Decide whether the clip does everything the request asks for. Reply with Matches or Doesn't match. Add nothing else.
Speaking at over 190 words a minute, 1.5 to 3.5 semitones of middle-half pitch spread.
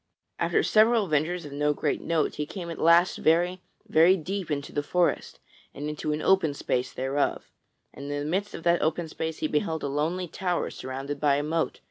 Matches